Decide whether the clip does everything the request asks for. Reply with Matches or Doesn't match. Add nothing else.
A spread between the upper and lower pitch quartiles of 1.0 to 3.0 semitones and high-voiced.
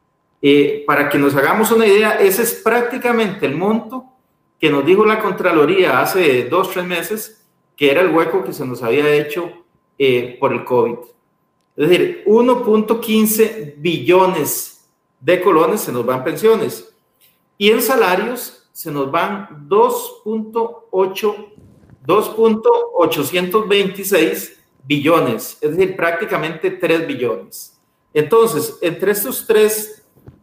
Doesn't match